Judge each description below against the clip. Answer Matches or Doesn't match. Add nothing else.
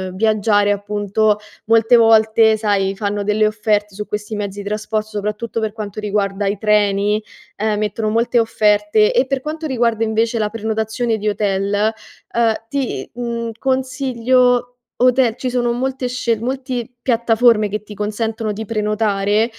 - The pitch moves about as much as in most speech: Doesn't match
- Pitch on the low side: Doesn't match